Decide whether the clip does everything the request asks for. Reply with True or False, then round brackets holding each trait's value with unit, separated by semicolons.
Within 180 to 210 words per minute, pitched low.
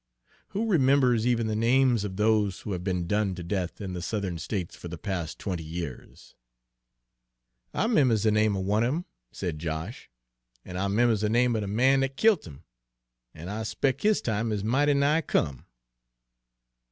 True (185 wpm; 105 Hz)